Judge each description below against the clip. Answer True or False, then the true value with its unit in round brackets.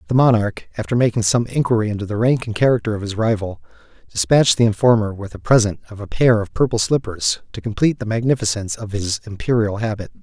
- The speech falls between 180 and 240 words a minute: True (200 wpm)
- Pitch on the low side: True (110 Hz)